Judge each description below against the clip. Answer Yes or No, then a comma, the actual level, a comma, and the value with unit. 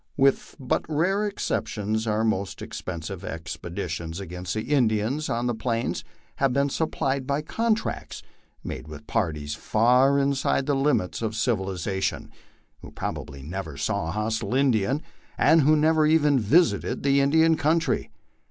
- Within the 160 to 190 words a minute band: No, average, 145 wpm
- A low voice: Yes, low, 120 Hz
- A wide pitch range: Yes, wide, 6.8 semitones